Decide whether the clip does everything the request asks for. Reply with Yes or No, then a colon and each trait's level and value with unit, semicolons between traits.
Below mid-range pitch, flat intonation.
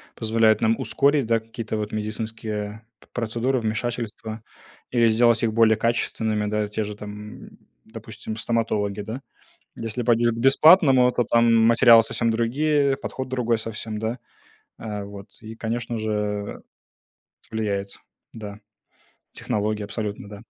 Yes: low, 110 Hz; narrow, 1.8 semitones